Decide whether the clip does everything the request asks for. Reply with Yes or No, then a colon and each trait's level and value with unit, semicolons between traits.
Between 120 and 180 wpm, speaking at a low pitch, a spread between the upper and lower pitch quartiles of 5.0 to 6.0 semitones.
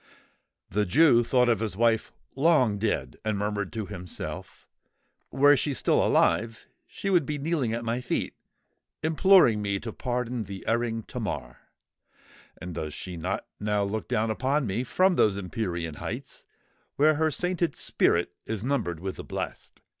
Yes: average, 155 wpm; low, 115 Hz; average, 5.3 semitones